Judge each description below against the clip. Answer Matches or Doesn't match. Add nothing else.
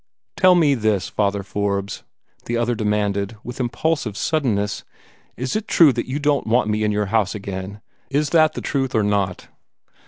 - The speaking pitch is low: Matches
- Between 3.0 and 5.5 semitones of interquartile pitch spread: Matches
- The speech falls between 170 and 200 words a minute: Matches